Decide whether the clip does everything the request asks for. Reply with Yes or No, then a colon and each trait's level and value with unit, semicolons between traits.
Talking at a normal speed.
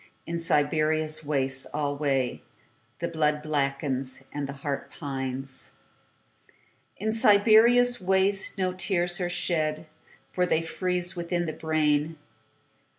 No: slow, 90 wpm